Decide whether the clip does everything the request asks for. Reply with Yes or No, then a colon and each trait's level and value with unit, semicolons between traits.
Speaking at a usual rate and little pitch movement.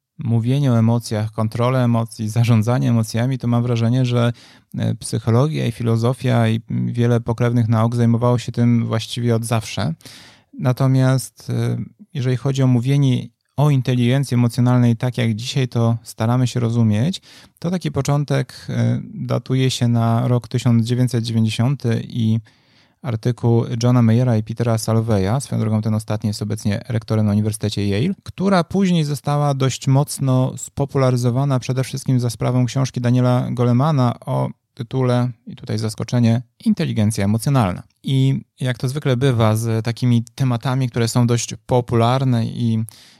Yes: average, 135 wpm; narrow, 2.2 semitones